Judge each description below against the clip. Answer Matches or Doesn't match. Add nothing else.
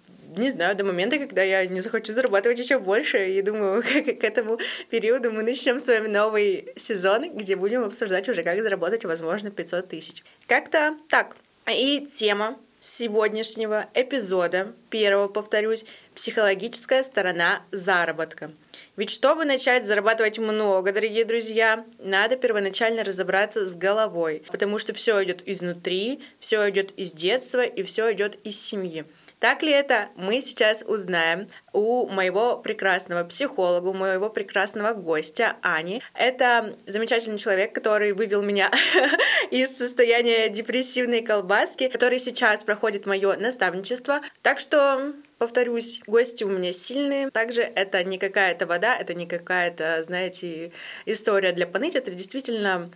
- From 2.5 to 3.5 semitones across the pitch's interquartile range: Doesn't match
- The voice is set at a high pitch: Matches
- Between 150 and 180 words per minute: Doesn't match